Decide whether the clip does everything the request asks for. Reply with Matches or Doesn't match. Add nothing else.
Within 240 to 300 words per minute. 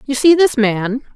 Doesn't match